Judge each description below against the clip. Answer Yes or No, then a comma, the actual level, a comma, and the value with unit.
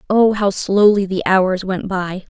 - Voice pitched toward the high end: Yes, high, 195 Hz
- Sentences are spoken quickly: No, average, 180 wpm